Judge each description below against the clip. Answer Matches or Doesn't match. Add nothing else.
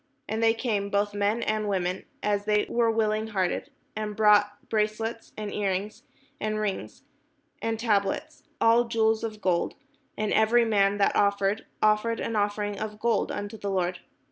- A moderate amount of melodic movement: Doesn't match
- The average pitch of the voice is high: Matches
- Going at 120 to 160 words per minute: Doesn't match